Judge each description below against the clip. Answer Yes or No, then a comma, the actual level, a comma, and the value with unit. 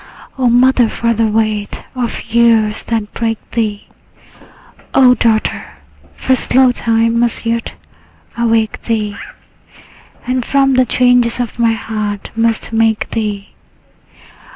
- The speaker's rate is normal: No, slow, 120 wpm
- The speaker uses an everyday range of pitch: No, narrow, 1.7 semitones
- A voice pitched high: Yes, high, 230 Hz